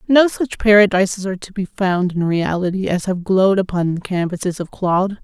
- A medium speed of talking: Yes, average, 195 wpm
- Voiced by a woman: Yes, female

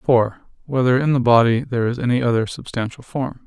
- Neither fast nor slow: Yes, average, 190 wpm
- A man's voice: Yes, male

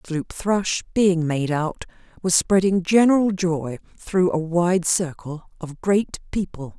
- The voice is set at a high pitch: No, medium, 175 Hz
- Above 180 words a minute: No, average, 140 wpm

